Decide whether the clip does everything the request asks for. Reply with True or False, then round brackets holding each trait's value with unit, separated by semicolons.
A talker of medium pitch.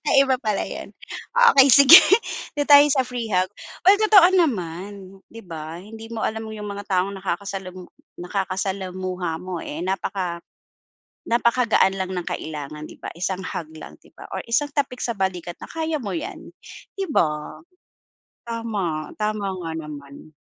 False (195 Hz)